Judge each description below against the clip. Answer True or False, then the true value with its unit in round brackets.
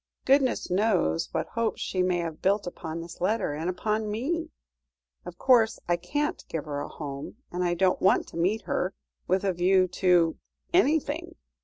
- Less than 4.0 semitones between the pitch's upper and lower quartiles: False (4.6 semitones)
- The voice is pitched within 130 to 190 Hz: True (185 Hz)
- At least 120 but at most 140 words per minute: False (175 wpm)